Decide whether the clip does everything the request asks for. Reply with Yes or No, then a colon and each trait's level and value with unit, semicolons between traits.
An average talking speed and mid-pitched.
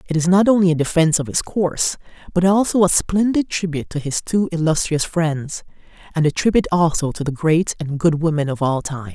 No: fast, 210 wpm; medium, 165 Hz